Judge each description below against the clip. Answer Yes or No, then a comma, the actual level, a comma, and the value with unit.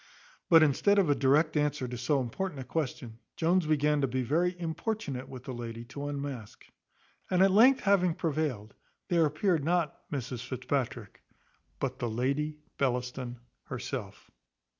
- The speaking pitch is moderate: Yes, medium, 145 Hz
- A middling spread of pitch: Yes, average, 4.6 semitones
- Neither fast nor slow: Yes, average, 150 wpm